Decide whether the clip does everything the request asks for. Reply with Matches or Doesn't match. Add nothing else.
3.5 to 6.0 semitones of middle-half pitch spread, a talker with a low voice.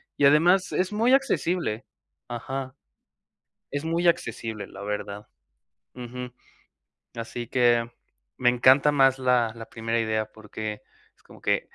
Matches